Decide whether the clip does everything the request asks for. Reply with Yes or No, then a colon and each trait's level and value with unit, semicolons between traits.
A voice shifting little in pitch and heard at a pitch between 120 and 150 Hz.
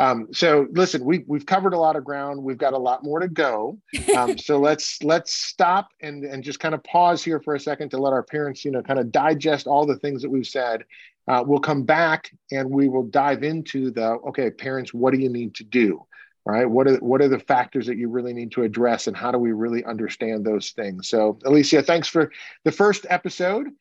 No: average, 3.8 semitones; medium, 140 Hz